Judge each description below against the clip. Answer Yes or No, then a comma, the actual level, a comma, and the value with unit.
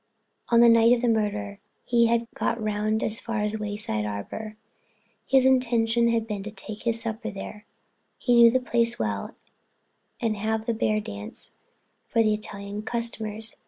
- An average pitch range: No, narrow, 1.9 semitones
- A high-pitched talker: Yes, high, 220 Hz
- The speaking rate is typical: Yes, average, 160 wpm